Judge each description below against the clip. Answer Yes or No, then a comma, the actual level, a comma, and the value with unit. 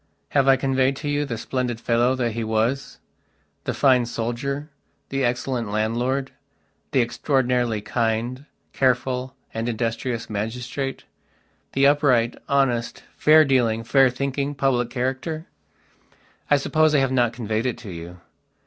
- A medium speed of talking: No, slow, 130 wpm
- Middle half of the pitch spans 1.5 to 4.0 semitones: Yes, average, 2.7 semitones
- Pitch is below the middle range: Yes, low, 125 Hz